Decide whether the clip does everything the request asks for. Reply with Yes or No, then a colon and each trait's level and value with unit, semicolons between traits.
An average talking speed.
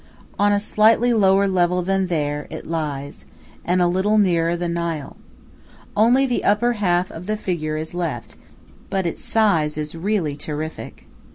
Yes: average, 160 wpm